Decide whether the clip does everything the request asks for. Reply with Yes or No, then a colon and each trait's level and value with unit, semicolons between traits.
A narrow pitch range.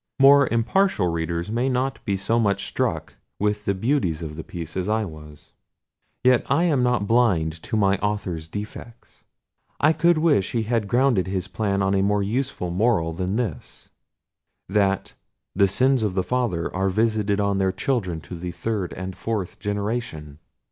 No: average, 4.5 semitones